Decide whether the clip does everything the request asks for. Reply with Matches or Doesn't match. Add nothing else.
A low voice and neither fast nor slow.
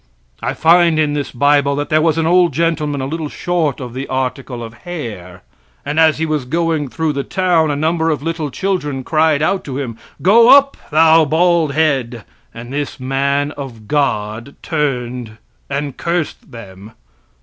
Doesn't match